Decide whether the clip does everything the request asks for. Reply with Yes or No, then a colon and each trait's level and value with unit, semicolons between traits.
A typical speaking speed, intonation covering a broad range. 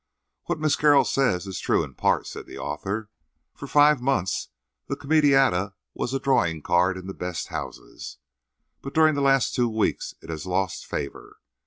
Yes: average, 175 wpm; wide, 7.4 semitones